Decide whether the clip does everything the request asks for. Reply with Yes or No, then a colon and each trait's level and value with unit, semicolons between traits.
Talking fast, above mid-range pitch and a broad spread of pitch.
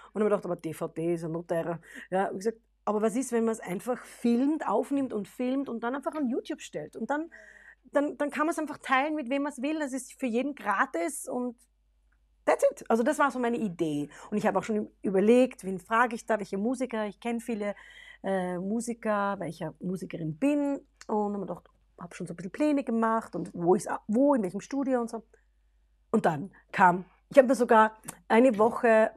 Yes: fast, 220 wpm; high, 225 Hz; wide, 5.8 semitones